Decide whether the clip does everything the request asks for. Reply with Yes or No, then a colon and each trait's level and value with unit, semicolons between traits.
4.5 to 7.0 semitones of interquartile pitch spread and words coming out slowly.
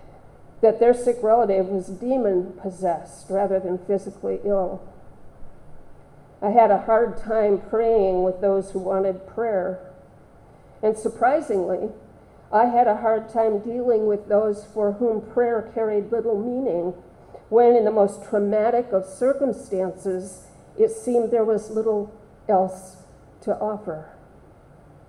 No: average, 3.0 semitones; slow, 125 wpm